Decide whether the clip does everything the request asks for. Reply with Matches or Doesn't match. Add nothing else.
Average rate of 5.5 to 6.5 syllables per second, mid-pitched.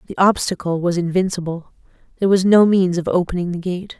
Matches